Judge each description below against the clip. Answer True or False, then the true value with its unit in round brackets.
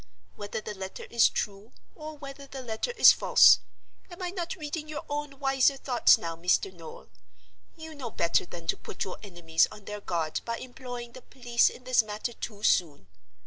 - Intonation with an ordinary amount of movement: False (7.4 semitones)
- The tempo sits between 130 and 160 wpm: False (180 wpm)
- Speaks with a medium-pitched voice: False (235 Hz)